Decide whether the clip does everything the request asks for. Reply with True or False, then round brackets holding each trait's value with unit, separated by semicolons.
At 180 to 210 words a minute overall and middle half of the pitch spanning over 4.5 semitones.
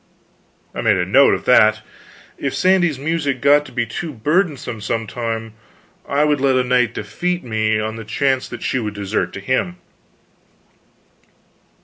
False (160 wpm; 5.0 semitones)